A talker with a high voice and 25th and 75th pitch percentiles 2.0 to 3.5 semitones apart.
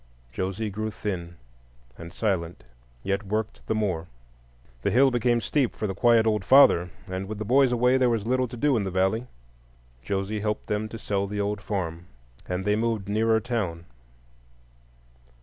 No: low, 105 Hz; average, 3.2 semitones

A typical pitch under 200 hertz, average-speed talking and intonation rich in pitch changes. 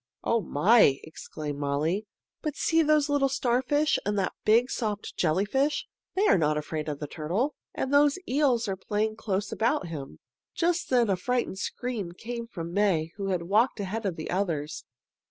No: high, 210 Hz; average, 170 wpm; wide, 6.9 semitones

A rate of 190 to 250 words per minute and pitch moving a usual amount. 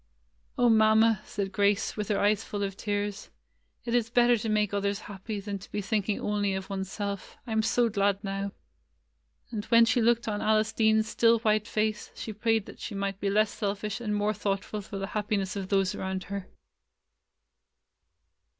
No: average, 195 wpm; narrow, 1.7 semitones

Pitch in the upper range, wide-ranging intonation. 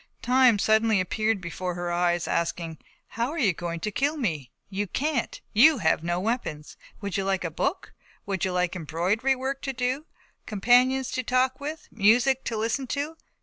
Yes: high, 220 Hz; wide, 6.5 semitones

